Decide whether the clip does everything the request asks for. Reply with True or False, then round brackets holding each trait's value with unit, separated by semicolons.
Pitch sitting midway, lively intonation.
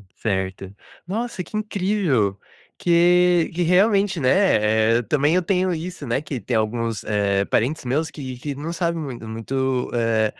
True (145 Hz; 7.5 semitones)